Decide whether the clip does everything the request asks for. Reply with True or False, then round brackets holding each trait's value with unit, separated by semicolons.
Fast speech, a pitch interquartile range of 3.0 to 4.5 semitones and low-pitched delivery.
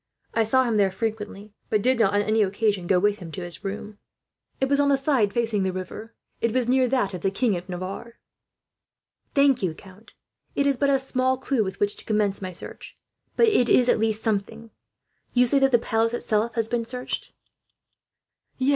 False (210 wpm; 4.1 semitones; 225 Hz)